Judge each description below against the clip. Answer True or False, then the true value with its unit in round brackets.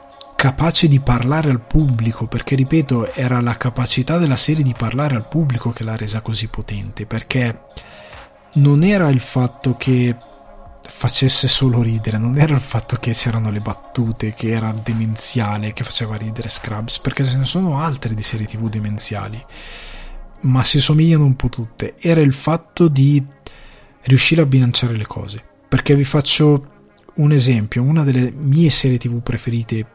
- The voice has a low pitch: True (125 Hz)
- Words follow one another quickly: False (160 wpm)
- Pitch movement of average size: True (3.7 semitones)